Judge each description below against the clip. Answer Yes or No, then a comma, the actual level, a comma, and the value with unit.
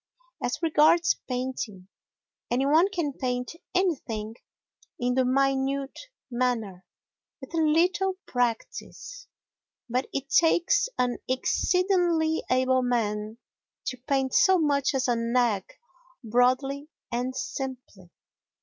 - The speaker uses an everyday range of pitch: Yes, average, 4.2 semitones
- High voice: Yes, very high, 260 Hz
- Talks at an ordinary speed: No, slow, 105 wpm